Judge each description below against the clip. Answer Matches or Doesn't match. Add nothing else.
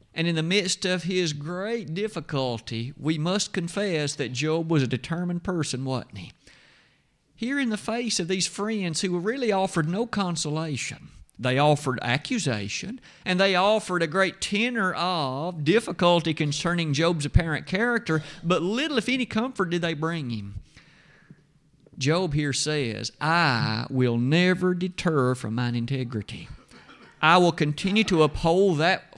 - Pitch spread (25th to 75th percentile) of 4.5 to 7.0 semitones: Matches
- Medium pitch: Matches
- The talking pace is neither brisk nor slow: Matches